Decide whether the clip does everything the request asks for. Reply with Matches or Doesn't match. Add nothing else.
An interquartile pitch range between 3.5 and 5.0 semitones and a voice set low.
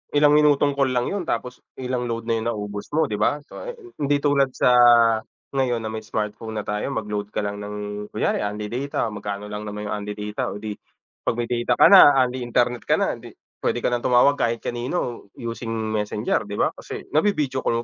Matches